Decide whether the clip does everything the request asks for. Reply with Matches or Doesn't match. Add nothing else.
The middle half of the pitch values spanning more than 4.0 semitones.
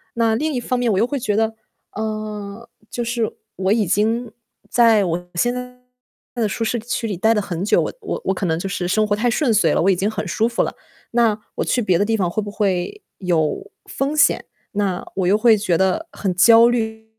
Doesn't match